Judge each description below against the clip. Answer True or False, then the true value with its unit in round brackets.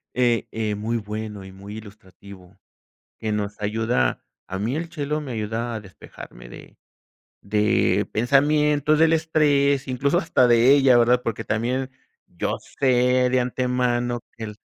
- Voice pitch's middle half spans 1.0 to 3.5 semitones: False (4.0 semitones)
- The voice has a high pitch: False (120 Hz)